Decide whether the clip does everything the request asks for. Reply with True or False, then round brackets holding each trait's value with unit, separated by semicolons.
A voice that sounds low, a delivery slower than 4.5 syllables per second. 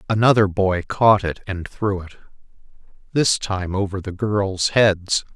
True (100 Hz; 3.9 syllables/s)